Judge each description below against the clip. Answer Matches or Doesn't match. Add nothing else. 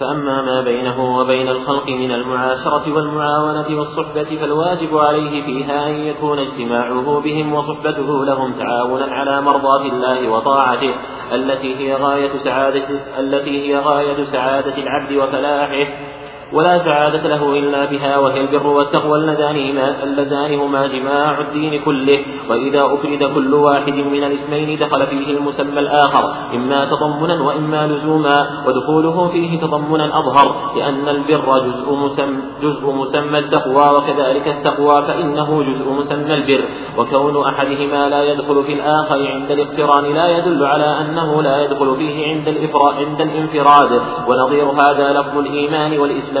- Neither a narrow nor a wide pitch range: Doesn't match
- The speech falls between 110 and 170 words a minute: Matches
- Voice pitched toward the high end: Doesn't match